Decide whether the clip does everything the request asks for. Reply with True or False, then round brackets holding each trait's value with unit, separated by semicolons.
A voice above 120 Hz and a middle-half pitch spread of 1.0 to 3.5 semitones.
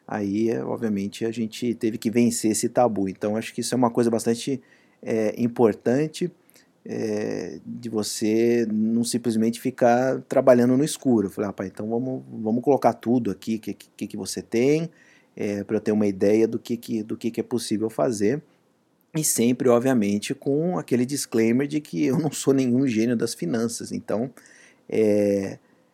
False (115 Hz; 2.6 semitones)